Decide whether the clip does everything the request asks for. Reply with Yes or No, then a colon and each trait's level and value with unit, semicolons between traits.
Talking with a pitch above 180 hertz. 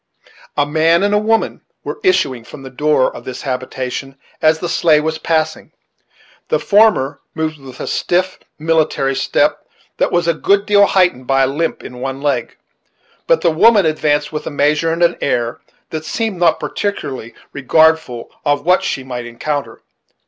No: medium, 155 Hz